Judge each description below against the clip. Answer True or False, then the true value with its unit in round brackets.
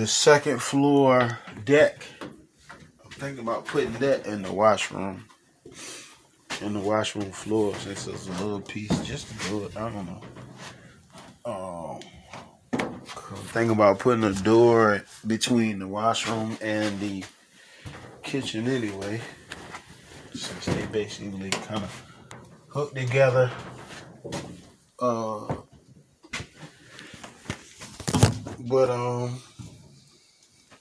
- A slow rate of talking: True (100 wpm)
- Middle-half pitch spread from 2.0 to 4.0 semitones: True (3.5 semitones)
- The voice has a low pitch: True (110 Hz)